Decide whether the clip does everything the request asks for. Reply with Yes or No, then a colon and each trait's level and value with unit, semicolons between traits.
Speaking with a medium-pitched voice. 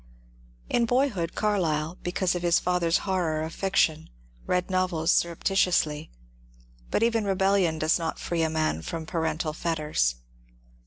Yes: medium, 170 Hz